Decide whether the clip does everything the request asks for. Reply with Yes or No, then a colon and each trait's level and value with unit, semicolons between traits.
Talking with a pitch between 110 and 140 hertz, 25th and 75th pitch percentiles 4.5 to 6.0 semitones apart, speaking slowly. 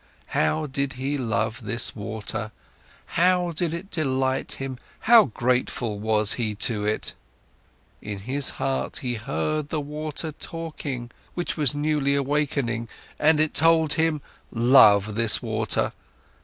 Yes: low, 135 Hz; average, 5.2 semitones; slow, 130 wpm